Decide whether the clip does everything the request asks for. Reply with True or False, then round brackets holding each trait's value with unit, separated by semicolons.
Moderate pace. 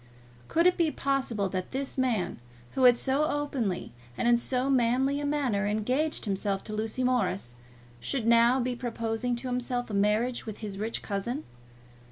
True (170 wpm)